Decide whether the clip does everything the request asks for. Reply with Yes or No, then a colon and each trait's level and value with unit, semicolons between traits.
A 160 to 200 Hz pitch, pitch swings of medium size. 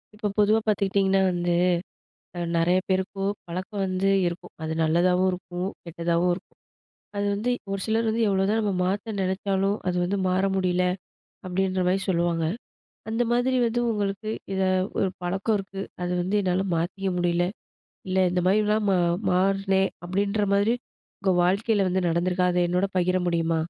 No: high, 190 Hz; narrow, 2.0 semitones